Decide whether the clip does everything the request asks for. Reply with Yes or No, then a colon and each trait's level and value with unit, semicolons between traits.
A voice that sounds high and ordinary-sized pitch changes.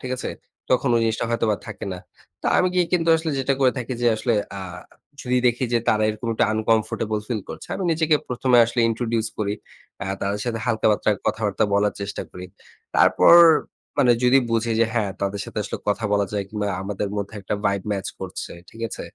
No: low, 110 Hz; average, 3.1 semitones